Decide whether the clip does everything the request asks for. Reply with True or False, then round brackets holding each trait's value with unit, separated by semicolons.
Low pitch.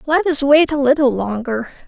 False (275 Hz)